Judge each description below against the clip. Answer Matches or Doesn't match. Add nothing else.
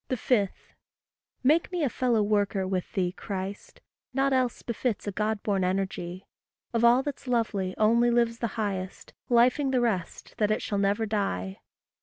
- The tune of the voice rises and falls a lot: Doesn't match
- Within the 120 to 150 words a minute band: Doesn't match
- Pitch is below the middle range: Doesn't match